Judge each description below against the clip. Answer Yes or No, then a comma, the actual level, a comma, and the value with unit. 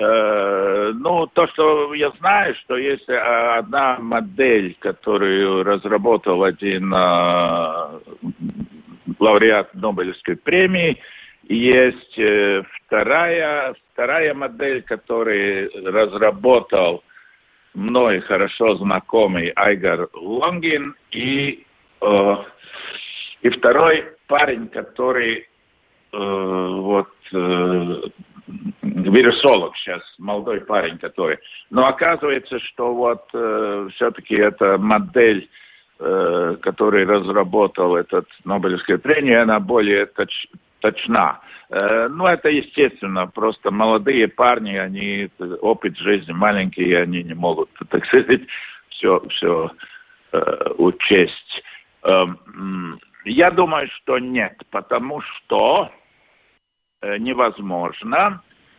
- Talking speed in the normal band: No, slow, 90 wpm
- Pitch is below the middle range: Yes, low, 115 Hz